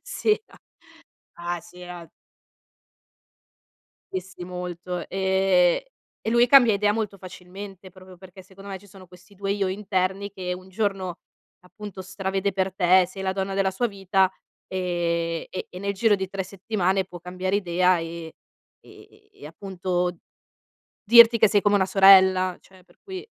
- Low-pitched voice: No, high, 190 Hz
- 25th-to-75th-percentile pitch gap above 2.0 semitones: No, narrow, 1.7 semitones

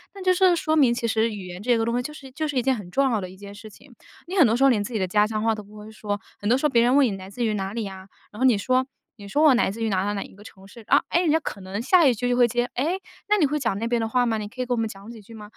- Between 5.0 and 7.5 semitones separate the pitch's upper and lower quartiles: No, average, 4.1 semitones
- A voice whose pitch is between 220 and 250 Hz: Yes, high, 230 Hz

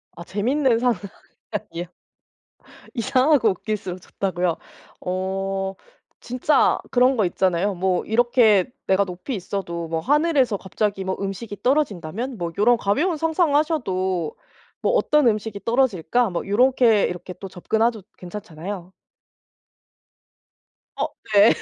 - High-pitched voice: Yes, high, 205 Hz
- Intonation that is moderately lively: Yes, average, 4.9 semitones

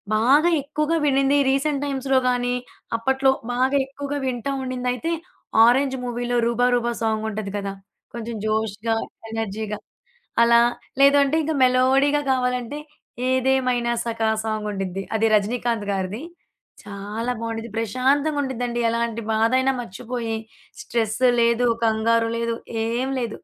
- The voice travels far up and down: No, average, 2.9 semitones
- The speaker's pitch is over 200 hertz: Yes, high, 240 Hz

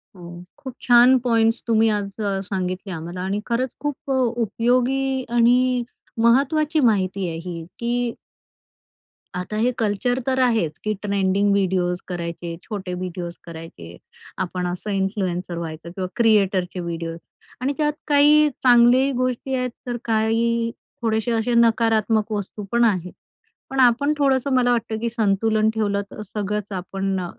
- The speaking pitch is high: Yes, high, 220 Hz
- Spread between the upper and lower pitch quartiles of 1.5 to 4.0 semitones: No, average, 4.7 semitones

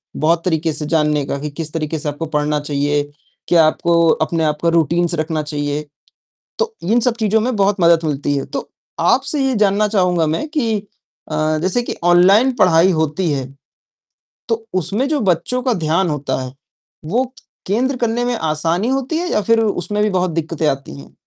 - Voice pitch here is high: No, medium, 170 Hz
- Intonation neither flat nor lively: No, wide, 5.9 semitones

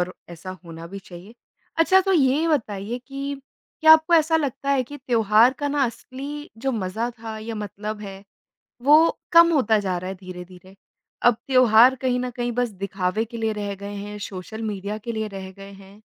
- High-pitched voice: Yes, high, 225 Hz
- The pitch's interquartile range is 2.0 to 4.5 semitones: No, average, 5.3 semitones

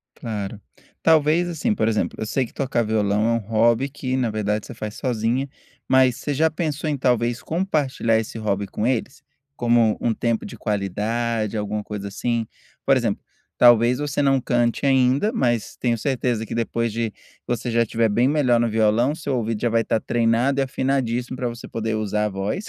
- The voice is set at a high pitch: No, low, 120 Hz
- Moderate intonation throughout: Yes, average, 3.2 semitones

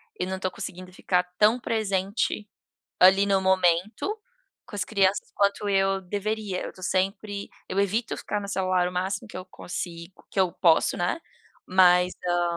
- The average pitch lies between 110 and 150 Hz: No, high, 190 Hz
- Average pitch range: No, narrow, 1.8 semitones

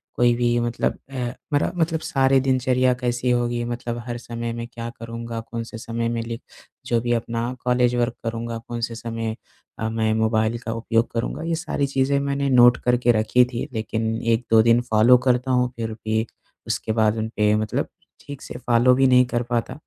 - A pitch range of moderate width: No, narrow, 1.5 semitones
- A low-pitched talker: Yes, low, 120 Hz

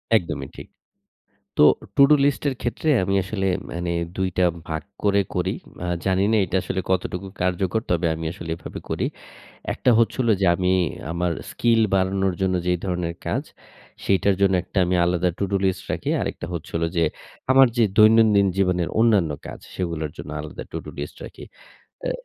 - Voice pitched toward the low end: Yes, very low, 95 Hz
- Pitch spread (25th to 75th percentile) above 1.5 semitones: Yes, narrow, 2.6 semitones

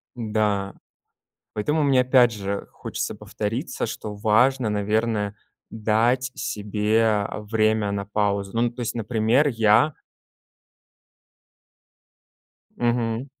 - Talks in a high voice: No, low, 110 Hz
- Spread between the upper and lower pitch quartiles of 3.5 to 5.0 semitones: No, narrow, 2.5 semitones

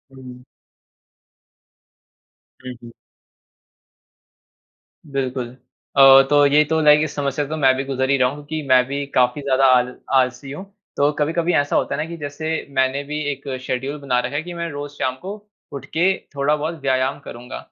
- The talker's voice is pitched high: No, medium, 140 Hz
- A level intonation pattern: Yes, narrow, 2.2 semitones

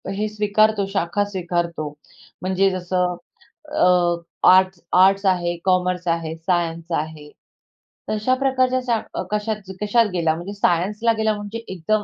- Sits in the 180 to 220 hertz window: Yes, medium, 185 Hz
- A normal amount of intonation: Yes, average, 3.4 semitones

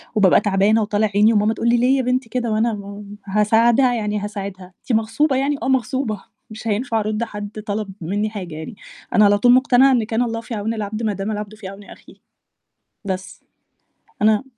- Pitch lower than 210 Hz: No, high, 215 Hz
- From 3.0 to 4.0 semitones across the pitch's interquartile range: No, narrow, 2.4 semitones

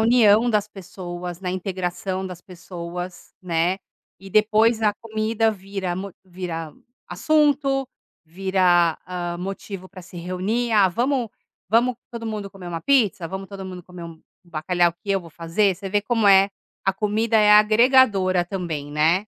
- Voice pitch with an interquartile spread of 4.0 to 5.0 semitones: No, average, 3.4 semitones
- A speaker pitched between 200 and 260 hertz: No, high, 190 Hz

